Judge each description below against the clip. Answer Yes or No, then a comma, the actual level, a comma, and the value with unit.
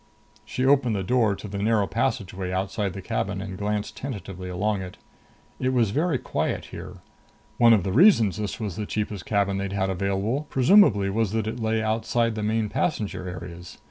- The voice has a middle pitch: No, low, 105 Hz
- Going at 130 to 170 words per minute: No, average, 185 wpm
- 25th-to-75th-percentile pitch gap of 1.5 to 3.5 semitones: Yes, average, 2.9 semitones